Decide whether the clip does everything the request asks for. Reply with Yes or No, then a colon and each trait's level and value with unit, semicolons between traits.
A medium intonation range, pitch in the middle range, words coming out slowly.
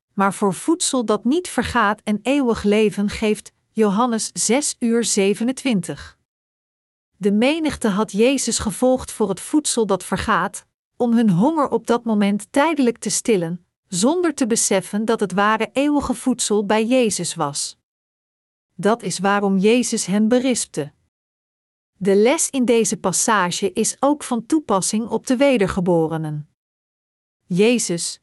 No: average, 4.1 semitones; high, 215 Hz; slow, 130 wpm